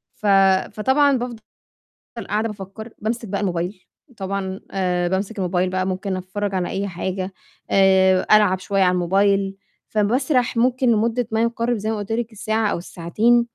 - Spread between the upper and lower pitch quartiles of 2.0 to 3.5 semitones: Yes, average, 3.1 semitones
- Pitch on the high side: Yes, high, 200 Hz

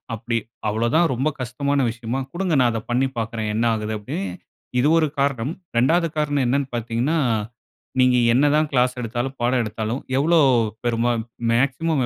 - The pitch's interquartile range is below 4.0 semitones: Yes, average, 3.5 semitones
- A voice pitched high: No, low, 125 Hz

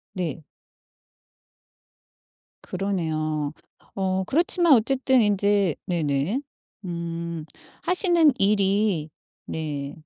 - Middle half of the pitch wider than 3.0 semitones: Yes, average, 5.2 semitones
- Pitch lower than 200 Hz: Yes, high, 190 Hz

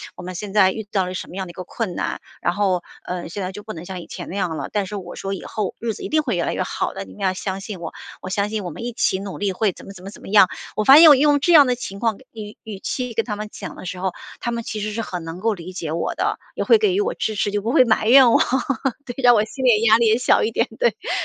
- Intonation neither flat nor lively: Yes, average, 3.9 semitones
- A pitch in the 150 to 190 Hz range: No, high, 205 Hz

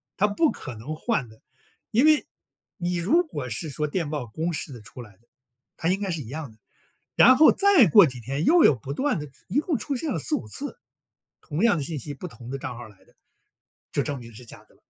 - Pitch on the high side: No, medium, 155 Hz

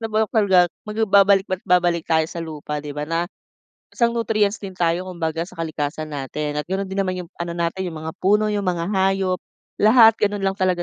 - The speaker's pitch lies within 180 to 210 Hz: Yes, medium, 185 Hz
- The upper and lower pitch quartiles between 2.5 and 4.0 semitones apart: Yes, average, 3.4 semitones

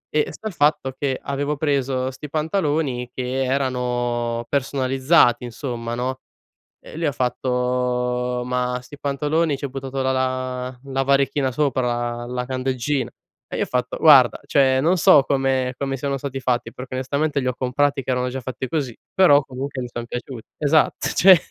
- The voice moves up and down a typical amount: No, narrow, 2.2 semitones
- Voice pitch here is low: Yes, low, 130 Hz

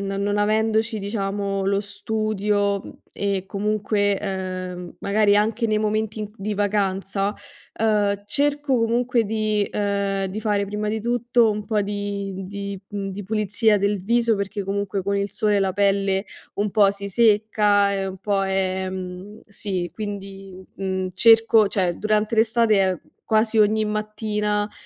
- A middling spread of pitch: No, narrow, 1.6 semitones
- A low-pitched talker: No, high, 205 Hz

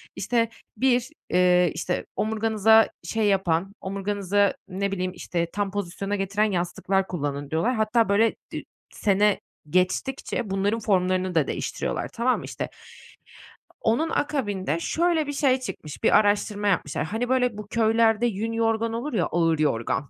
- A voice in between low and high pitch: No, high, 205 Hz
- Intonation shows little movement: No, average, 3.7 semitones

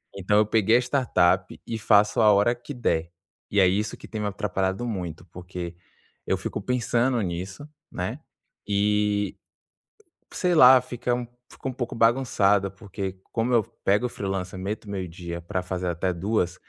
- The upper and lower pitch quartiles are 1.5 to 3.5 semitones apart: No, average, 4.1 semitones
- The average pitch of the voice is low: Yes, low, 105 Hz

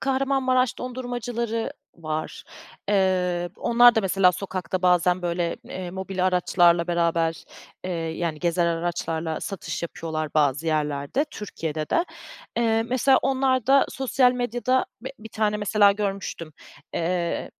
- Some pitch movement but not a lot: No, wide, 5.9 semitones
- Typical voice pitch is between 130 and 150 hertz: No, medium, 185 Hz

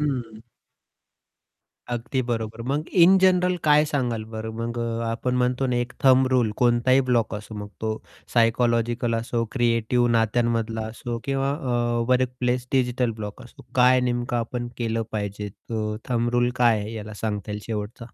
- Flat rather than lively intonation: Yes, narrow, 1.9 semitones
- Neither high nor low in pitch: No, low, 120 Hz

